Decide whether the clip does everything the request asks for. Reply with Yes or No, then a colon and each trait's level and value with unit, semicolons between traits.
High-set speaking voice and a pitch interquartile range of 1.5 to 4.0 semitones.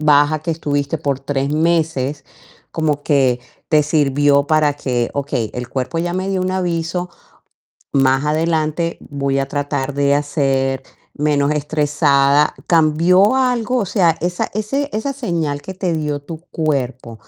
No: medium, 150 Hz; average, 3.2 semitones